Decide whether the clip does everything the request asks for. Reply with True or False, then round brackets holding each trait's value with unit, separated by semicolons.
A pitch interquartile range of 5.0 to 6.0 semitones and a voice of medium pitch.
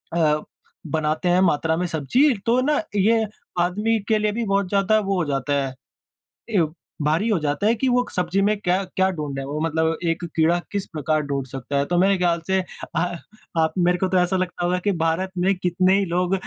False (3.8 semitones; 180 Hz)